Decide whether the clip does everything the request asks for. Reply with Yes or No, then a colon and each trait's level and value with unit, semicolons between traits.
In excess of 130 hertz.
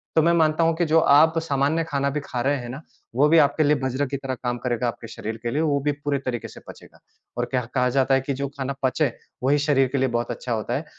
Yes: medium, 140 Hz